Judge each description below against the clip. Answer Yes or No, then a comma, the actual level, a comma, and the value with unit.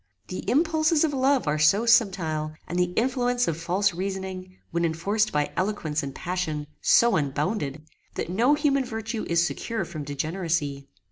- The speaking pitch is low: No, medium, 185 Hz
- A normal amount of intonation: No, wide, 6.7 semitones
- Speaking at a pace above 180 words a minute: No, average, 155 wpm